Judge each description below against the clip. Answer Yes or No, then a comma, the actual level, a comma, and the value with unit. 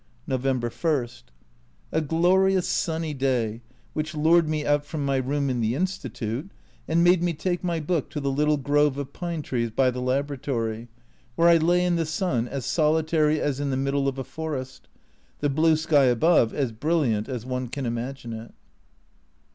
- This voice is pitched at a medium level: Yes, medium, 145 Hz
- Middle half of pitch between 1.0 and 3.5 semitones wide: No, average, 3.9 semitones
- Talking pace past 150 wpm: Yes, average, 180 wpm